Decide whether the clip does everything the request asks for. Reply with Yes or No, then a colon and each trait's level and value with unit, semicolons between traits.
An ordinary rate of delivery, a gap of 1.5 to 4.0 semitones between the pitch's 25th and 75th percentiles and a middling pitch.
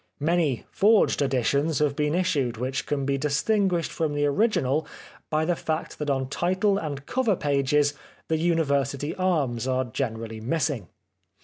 Yes: average, 145 wpm; average, 3.5 semitones; medium, 145 Hz